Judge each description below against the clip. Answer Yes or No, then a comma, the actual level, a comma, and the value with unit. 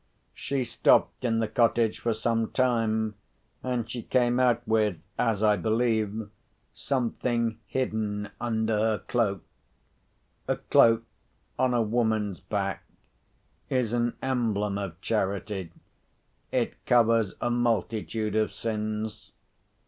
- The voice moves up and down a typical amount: No, narrow, 2.0 semitones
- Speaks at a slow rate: Yes, slow, 110 wpm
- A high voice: No, low, 110 Hz